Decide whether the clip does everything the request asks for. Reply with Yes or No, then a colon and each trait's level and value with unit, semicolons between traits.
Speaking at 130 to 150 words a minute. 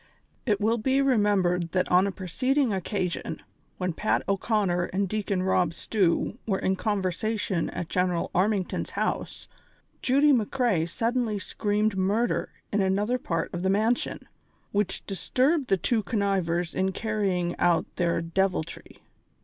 Yes: average, 140 wpm